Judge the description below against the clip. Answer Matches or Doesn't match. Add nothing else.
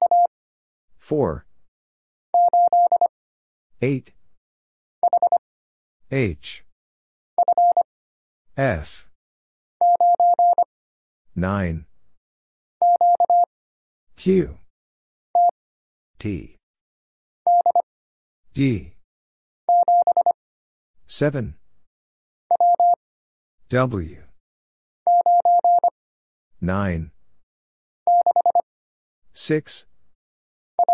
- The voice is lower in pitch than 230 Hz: Matches